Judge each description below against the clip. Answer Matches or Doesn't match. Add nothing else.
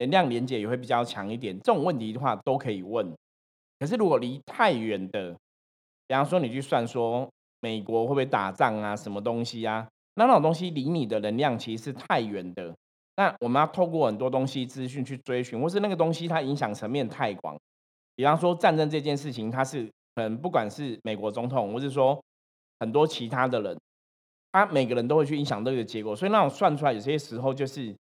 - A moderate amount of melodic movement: Matches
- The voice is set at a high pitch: Doesn't match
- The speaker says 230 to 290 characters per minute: Doesn't match